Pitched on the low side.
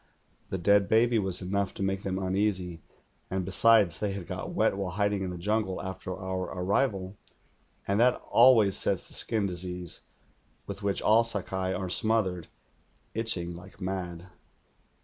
Yes: very low, 95 Hz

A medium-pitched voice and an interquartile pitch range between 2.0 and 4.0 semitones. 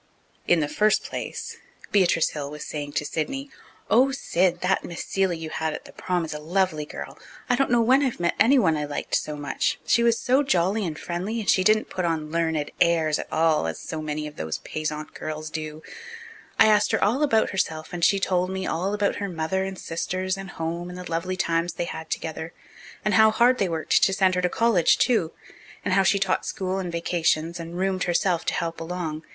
Yes: medium, 175 Hz; average, 3.5 semitones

